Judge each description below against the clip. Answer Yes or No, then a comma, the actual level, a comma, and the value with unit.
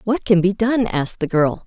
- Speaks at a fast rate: Yes, fast, 250 wpm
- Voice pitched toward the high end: Yes, high, 195 Hz